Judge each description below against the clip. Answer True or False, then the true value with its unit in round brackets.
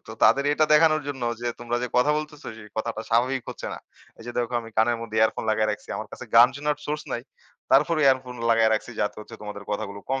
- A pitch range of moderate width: True (3.9 semitones)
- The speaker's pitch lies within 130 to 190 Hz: False (120 Hz)